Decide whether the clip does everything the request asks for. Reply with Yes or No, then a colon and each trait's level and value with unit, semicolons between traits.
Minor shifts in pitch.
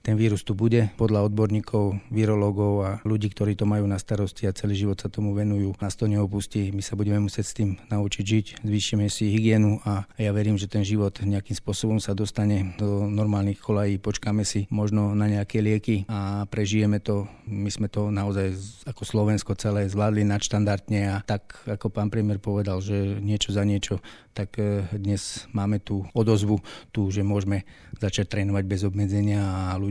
Yes: narrow, 0.9 semitones